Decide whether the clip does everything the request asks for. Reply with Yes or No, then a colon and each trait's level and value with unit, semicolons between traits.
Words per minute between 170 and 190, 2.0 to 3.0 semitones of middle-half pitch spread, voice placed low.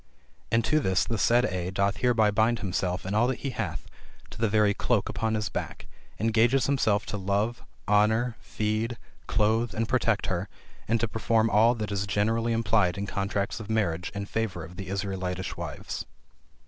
Yes: average, 180 wpm; narrow, 2.6 semitones; low, 105 Hz